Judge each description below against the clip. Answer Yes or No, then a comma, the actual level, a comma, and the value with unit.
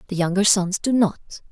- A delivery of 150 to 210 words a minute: Yes, average, 200 wpm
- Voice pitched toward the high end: Yes, high, 195 Hz